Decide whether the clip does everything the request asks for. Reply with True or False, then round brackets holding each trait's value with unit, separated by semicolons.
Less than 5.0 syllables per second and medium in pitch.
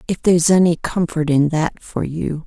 True (4.8 syllables/s; 165 Hz)